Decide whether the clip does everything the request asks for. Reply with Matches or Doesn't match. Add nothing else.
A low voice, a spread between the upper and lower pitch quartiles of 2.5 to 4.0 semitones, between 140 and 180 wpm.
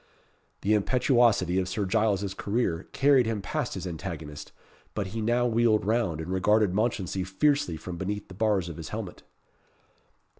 Matches